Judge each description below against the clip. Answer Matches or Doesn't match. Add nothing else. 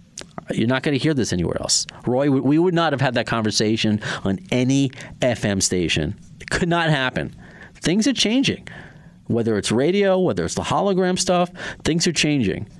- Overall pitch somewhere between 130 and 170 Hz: Matches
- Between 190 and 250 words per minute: Doesn't match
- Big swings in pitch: Matches